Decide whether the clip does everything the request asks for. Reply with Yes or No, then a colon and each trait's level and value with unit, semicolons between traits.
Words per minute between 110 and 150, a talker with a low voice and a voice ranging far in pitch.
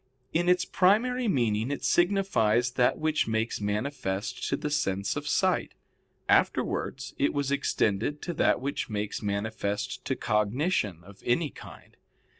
Yes: average, 140 wpm; low, 125 Hz; wide, 6.7 semitones